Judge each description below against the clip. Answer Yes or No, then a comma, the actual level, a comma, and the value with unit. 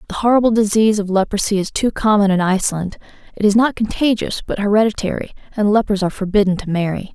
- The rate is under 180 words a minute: No, average, 185 wpm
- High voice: Yes, high, 205 Hz